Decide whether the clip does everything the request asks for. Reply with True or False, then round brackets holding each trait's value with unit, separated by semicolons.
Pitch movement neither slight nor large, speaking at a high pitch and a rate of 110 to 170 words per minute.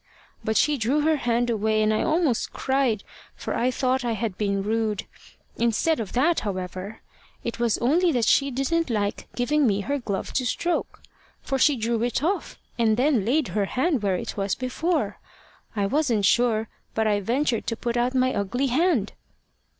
False (4.3 semitones; 240 Hz; 180 wpm)